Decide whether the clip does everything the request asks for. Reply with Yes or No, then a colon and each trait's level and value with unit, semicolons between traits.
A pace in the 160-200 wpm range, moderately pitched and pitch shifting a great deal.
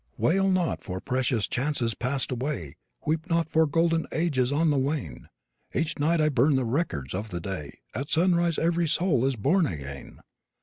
Yes: average, 175 wpm; medium, 145 Hz; wide, 5.9 semitones